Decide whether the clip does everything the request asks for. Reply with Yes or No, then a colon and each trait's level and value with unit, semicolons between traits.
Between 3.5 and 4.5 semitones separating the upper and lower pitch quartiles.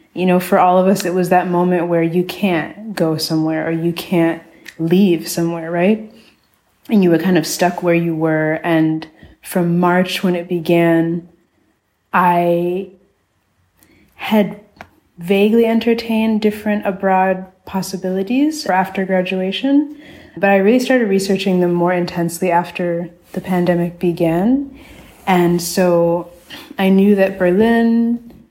No: narrow, 2.6 semitones